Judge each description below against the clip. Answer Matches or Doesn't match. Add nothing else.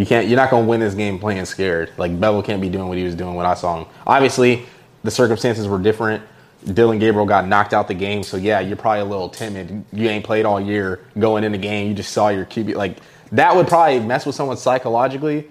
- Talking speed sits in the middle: Doesn't match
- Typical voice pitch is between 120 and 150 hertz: Doesn't match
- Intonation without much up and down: Doesn't match